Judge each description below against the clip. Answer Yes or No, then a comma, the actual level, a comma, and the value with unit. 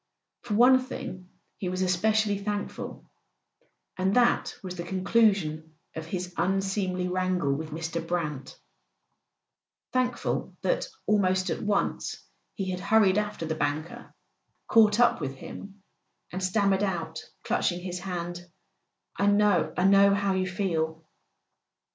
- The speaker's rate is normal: No, slow, 125 wpm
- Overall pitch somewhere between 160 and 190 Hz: Yes, medium, 185 Hz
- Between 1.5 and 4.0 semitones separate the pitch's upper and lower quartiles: Yes, average, 2.7 semitones